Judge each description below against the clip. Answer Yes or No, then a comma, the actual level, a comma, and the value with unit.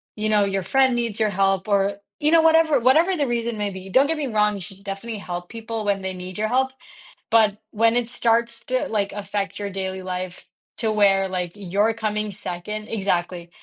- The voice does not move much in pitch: No, average, 3.2 semitones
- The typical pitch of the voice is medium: No, high, 210 Hz